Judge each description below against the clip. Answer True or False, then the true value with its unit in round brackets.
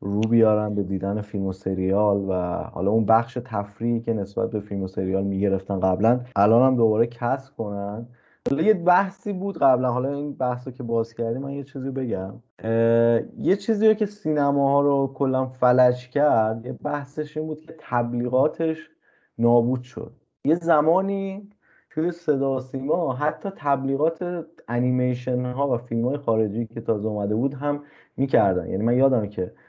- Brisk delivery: True (160 wpm)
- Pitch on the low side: True (125 Hz)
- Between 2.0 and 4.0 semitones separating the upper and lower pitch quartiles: False (4.5 semitones)